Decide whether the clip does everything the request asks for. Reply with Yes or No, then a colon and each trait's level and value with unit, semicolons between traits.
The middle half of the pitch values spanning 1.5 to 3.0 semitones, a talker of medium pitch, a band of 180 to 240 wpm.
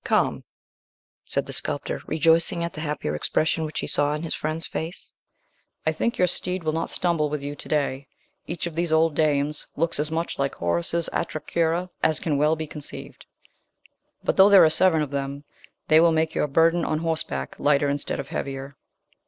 Yes: narrow, 2.4 semitones; medium, 155 Hz; average, 195 wpm